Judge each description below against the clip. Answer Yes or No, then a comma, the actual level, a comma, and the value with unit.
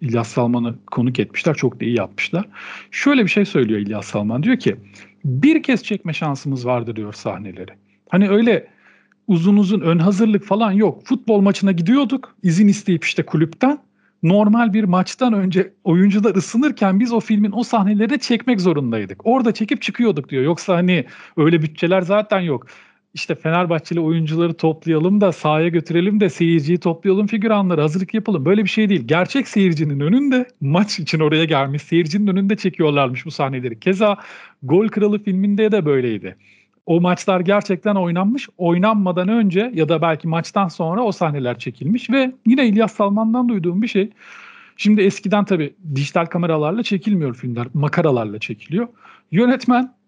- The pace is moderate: No, fast, 155 wpm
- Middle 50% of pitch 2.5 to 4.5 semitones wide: No, average, 5.2 semitones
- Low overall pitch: No, medium, 185 Hz